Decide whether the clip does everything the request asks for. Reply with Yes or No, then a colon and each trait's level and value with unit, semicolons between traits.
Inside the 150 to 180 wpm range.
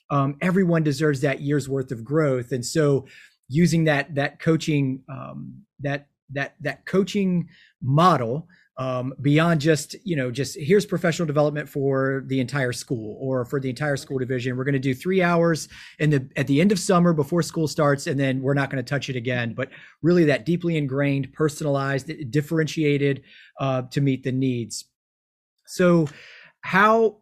Yes: average, 170 wpm